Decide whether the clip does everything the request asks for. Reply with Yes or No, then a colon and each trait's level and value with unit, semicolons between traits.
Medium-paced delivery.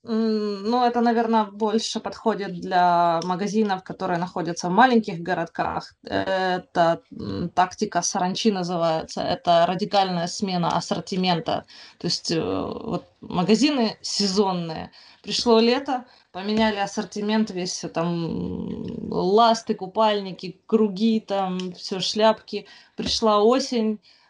No: slow, 95 wpm